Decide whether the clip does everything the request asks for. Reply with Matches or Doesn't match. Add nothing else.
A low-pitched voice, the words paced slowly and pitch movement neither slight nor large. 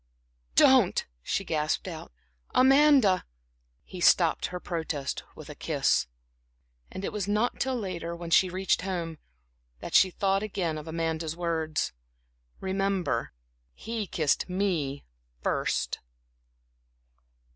Doesn't match